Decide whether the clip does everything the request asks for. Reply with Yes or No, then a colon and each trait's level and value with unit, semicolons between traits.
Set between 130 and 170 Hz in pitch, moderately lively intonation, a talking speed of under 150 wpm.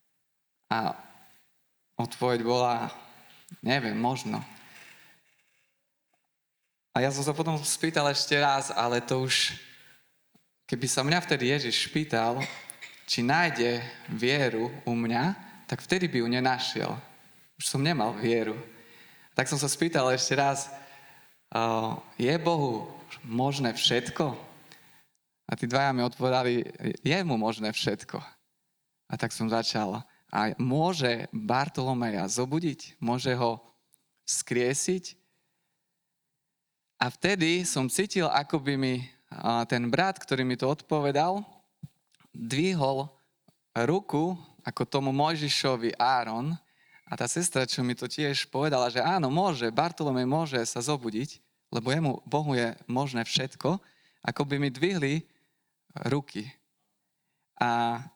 Yes: low, 135 Hz; average, 4.6 semitones; average, 115 wpm